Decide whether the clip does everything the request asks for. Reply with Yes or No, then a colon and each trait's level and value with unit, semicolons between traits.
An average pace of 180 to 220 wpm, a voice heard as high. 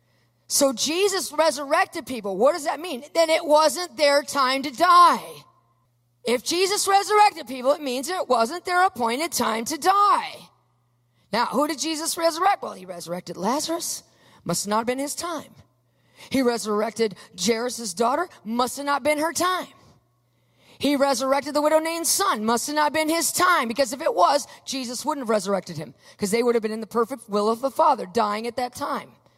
Yes: average, 185 wpm; very high, 275 Hz